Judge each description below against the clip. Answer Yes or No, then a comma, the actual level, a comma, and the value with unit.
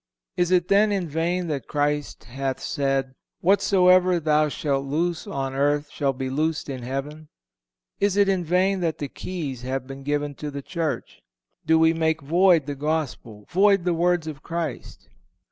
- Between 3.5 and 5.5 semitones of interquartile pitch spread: Yes, average, 4.2 semitones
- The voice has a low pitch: No, medium, 155 Hz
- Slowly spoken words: No, average, 170 wpm